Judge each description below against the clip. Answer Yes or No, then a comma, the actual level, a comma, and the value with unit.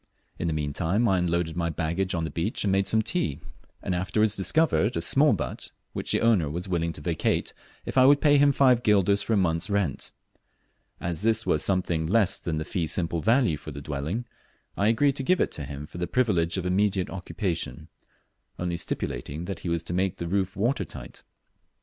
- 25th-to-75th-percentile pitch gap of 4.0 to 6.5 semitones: Yes, average, 4.6 semitones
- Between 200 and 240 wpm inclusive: Yes, fast, 205 wpm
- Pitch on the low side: Yes, very low, 90 Hz